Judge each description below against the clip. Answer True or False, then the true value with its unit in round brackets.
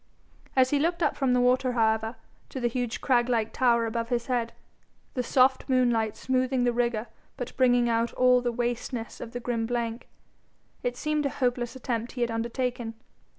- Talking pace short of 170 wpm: False (185 wpm)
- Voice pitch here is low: False (245 Hz)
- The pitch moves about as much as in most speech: False (1.5 semitones)